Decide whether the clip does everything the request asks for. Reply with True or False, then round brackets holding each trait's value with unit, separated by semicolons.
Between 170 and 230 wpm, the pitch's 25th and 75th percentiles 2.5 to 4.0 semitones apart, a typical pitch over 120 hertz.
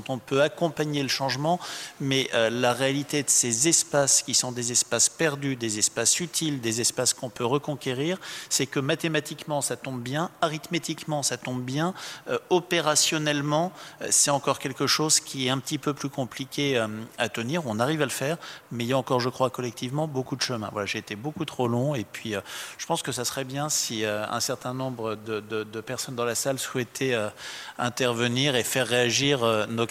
True (210 wpm; 3.6 semitones; 135 Hz)